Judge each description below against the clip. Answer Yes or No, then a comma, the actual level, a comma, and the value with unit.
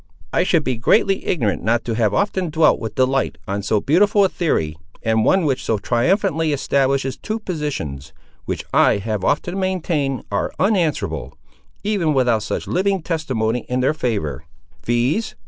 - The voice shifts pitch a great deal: Yes, wide, 8.0 semitones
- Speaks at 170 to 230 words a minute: No, average, 155 wpm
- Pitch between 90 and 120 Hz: No, low, 135 Hz